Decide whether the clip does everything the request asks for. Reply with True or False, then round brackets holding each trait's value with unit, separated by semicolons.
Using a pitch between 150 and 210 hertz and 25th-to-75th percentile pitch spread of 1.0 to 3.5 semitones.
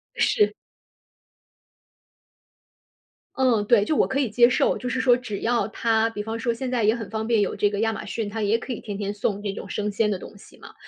False (225 Hz; 2.6 semitones)